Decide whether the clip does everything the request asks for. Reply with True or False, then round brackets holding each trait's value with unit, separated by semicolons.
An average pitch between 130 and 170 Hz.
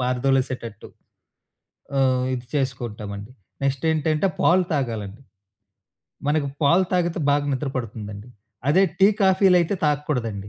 True (135 Hz)